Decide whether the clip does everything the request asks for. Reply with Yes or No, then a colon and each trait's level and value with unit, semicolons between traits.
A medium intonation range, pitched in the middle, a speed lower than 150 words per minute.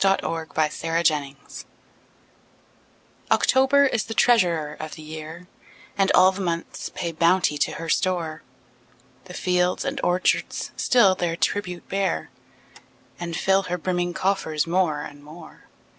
Yes: average, 3.0 semitones; medium, 175 Hz; slow, 135 wpm